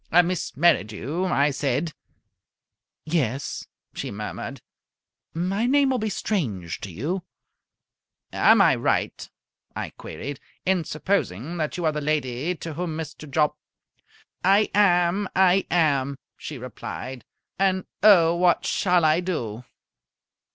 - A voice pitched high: No, medium, 165 Hz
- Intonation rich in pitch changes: No, average, 4.7 semitones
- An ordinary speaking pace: No, slow, 125 wpm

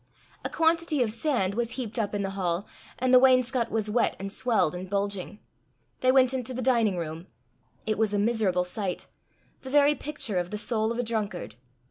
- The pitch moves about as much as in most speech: Yes, average, 4.4 semitones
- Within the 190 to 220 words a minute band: Yes, average, 195 wpm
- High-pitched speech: Yes, high, 220 Hz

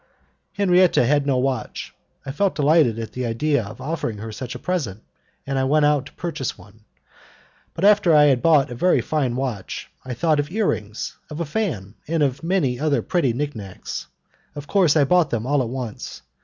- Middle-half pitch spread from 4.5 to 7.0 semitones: Yes, average, 4.8 semitones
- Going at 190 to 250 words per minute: Yes, average, 195 wpm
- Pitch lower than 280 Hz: Yes, medium, 140 Hz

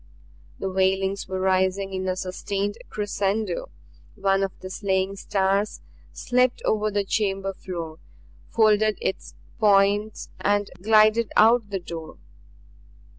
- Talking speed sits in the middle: No, slow, 120 wpm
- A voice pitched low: No, high, 195 Hz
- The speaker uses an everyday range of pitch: No, narrow, 1.9 semitones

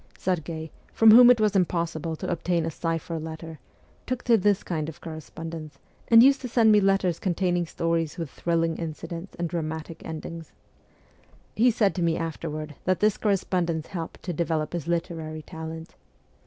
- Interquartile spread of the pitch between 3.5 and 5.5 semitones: No, average, 2.8 semitones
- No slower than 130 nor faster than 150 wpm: No, average, 165 wpm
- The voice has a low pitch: No, medium, 165 Hz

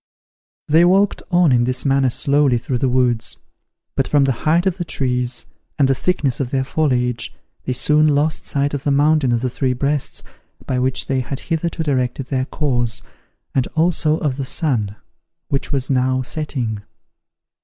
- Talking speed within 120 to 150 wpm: No, average, 175 wpm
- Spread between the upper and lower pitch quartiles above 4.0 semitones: No, average, 3.1 semitones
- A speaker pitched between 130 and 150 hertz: Yes, low, 135 Hz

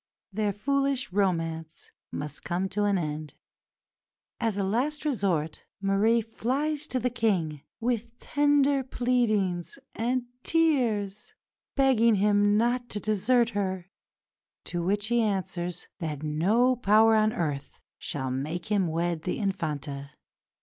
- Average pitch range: No, wide, 5.7 semitones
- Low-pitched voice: No, high, 205 Hz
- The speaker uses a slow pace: Yes, slow, 125 wpm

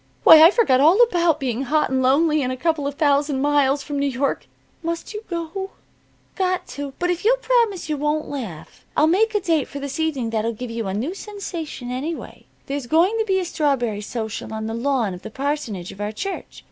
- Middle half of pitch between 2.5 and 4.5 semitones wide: No, average, 5.0 semitones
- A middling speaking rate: No, fast, 215 wpm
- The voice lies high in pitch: Yes, very high, 290 Hz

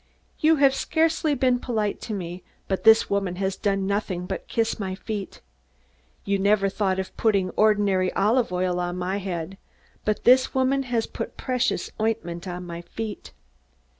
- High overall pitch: Yes, high, 200 Hz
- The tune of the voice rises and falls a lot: No, average, 3.8 semitones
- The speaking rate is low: No, average, 165 wpm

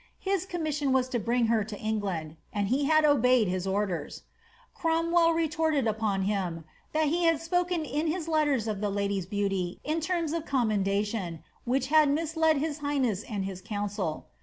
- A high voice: Yes, very high, 250 Hz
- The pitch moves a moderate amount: No, wide, 7.6 semitones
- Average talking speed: Yes, average, 175 wpm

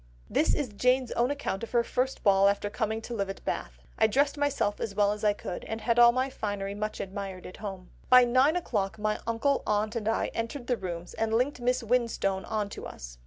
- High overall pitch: Yes, high, 220 Hz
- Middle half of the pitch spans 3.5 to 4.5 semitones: Yes, average, 3.8 semitones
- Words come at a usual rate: No, fast, 225 wpm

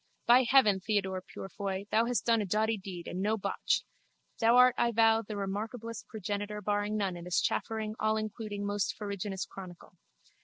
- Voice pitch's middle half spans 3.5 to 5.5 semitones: No, narrow, 2.4 semitones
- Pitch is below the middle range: No, high, 210 Hz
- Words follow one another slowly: No, average, 165 wpm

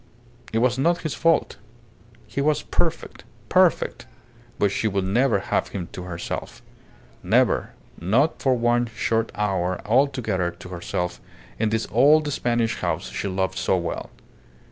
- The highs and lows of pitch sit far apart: Yes, wide, 5.7 semitones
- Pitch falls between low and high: No, low, 110 Hz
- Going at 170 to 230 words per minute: No, average, 145 wpm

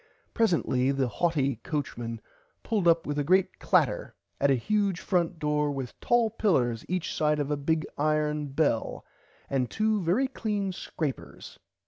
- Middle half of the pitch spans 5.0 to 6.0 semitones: Yes, average, 5.3 semitones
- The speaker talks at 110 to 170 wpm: Yes, average, 145 wpm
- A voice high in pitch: No, medium, 155 Hz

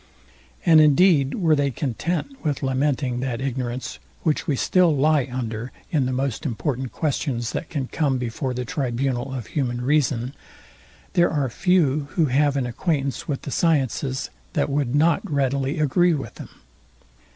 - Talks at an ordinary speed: Yes, average, 155 wpm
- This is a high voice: No, medium, 140 Hz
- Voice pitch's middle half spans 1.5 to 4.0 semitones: Yes, average, 3.1 semitones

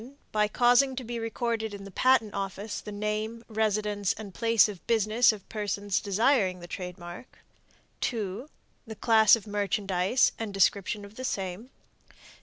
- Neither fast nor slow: Yes, average, 150 wpm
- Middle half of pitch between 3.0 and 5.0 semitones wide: No, narrow, 2.5 semitones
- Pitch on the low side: No, high, 210 Hz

